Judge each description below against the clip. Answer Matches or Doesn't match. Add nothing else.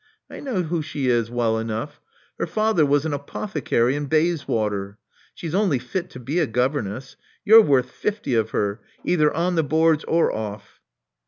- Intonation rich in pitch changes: Matches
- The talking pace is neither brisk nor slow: Matches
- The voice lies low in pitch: Doesn't match